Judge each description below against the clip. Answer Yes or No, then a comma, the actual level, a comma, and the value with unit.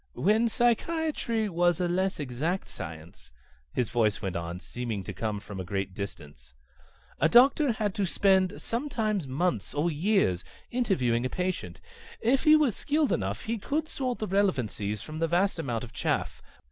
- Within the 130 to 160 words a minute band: No, average, 170 wpm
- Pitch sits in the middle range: Yes, medium, 175 Hz